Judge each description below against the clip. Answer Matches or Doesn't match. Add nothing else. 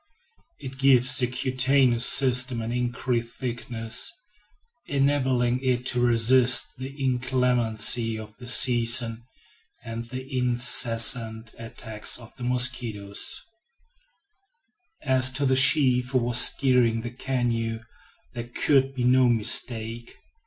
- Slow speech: Matches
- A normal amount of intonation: Doesn't match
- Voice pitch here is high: Doesn't match